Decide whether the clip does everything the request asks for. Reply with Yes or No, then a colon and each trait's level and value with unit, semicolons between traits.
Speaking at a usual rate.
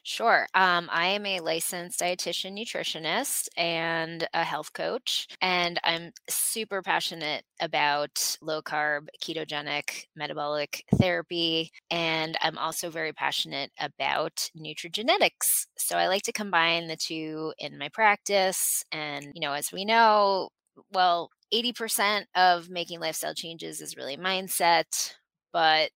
No: slow, 125 wpm